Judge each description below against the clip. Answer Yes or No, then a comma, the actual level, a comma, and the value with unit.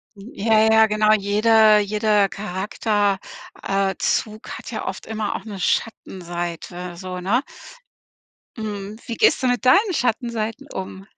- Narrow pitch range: Yes, narrow, 2.2 semitones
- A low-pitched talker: No, high, 210 Hz